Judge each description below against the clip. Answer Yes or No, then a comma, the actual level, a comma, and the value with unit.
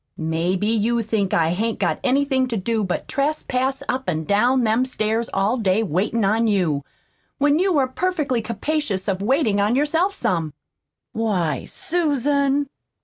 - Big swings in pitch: Yes, wide, 5.7 semitones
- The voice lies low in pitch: No, high, 230 Hz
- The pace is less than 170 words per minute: Yes, average, 150 wpm